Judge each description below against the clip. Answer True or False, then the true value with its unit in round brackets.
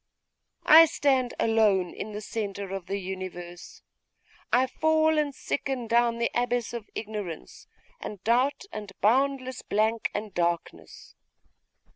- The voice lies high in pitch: True (225 Hz)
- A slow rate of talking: True (125 wpm)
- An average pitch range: True (4.5 semitones)